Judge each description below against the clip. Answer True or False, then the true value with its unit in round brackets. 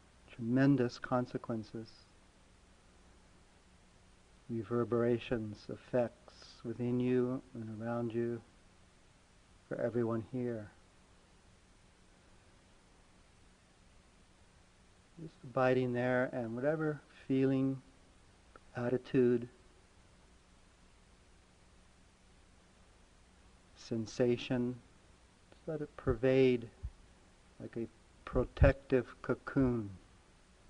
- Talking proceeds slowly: True (55 wpm)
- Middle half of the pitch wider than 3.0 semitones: True (5.2 semitones)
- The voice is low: True (110 Hz)